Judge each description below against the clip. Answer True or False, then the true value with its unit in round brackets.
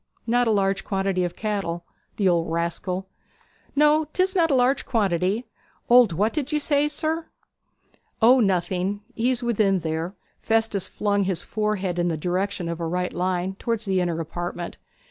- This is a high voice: True (195 Hz)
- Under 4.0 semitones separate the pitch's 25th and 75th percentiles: False (5.1 semitones)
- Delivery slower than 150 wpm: False (165 wpm)